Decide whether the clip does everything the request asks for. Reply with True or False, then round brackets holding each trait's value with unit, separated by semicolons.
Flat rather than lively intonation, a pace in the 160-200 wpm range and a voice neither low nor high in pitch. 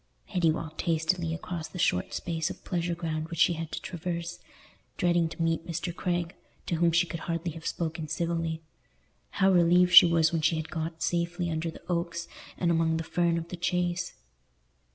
True (1.3 semitones; 190 wpm; 170 Hz)